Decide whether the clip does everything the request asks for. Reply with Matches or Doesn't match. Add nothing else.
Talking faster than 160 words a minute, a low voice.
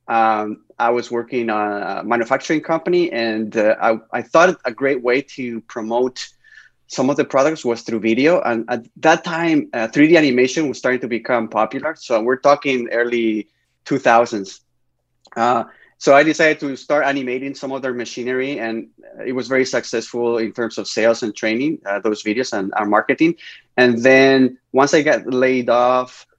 Matches